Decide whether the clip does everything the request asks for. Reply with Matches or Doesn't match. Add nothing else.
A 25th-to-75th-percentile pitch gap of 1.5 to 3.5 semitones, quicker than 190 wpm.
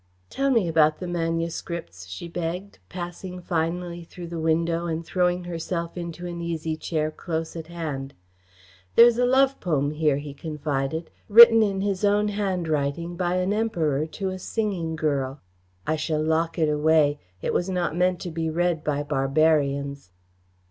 Doesn't match